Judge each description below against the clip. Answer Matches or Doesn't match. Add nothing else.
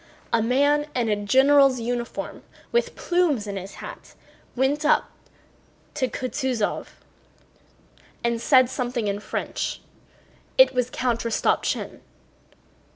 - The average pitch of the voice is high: Matches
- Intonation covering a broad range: Doesn't match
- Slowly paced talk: Matches